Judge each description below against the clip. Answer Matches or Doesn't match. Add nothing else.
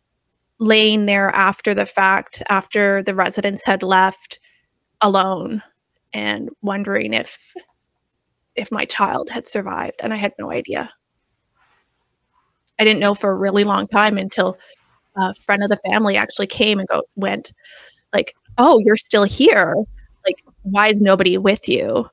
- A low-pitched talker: Doesn't match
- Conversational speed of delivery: Matches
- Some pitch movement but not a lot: Doesn't match